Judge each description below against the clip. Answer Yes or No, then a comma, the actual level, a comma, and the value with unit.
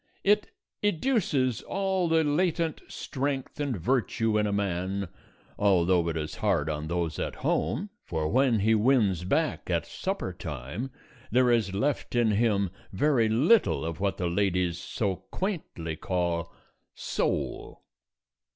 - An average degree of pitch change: No, wide, 8.2 semitones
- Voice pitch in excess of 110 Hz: No, low, 105 Hz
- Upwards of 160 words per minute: No, slow, 135 wpm